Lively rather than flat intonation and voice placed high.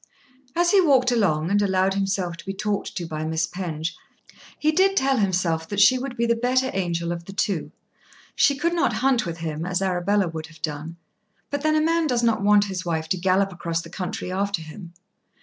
Yes: wide, 6.3 semitones; high, 195 Hz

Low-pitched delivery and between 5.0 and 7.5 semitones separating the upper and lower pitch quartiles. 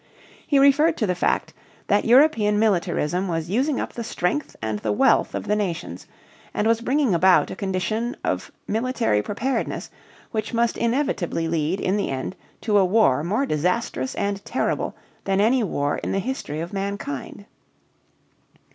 No: high, 205 Hz; average, 5.3 semitones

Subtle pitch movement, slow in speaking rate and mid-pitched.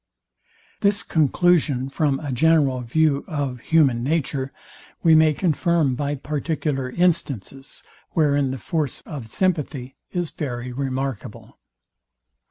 No: average, 3.3 semitones; slow, 110 wpm; medium, 145 Hz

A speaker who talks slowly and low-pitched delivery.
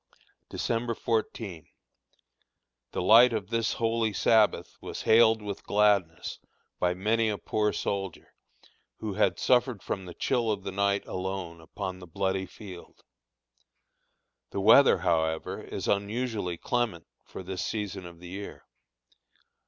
Yes: slow, 130 wpm; low, 100 Hz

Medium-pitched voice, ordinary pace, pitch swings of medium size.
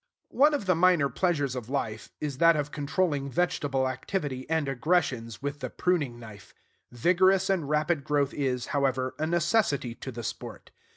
Yes: medium, 145 Hz; average, 165 wpm; average, 4.9 semitones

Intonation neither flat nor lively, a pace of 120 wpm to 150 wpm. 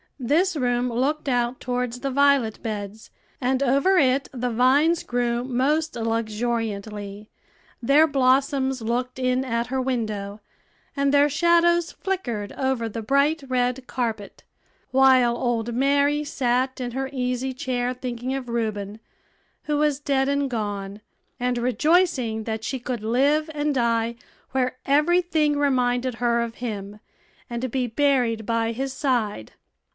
Yes: average, 3.1 semitones; average, 140 wpm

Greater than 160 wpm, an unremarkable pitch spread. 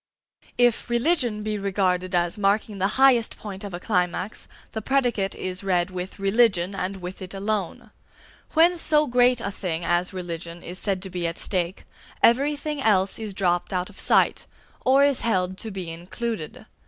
Yes: average, 170 wpm; average, 4.4 semitones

